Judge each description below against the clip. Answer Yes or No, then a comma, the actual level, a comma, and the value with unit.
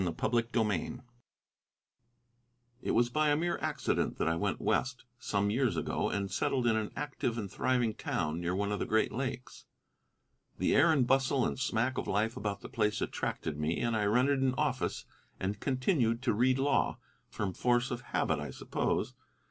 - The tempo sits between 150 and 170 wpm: No, average, 180 wpm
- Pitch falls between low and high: No, low, 120 Hz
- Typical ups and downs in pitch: Yes, average, 4.0 semitones